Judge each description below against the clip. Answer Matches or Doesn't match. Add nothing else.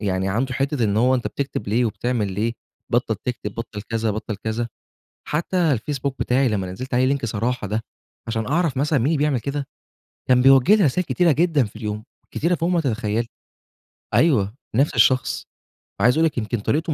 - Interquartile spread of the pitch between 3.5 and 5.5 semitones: Matches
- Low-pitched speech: Matches